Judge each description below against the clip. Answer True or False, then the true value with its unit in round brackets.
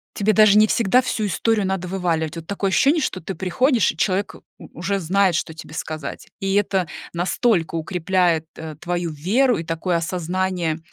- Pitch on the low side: False (185 Hz)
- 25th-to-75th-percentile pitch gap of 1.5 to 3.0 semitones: False (3.4 semitones)